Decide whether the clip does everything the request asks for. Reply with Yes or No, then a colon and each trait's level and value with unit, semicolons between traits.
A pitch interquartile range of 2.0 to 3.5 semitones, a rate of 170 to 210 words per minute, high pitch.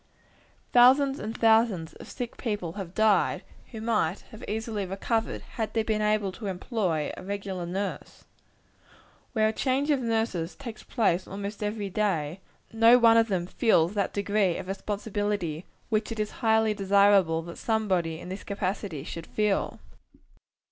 No: average, 3.1 semitones; average, 155 wpm; high, 205 Hz